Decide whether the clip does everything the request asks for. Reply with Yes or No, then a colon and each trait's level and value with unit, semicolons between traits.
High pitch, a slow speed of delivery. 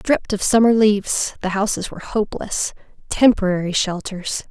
Yes: high, 205 Hz; slow, 120 wpm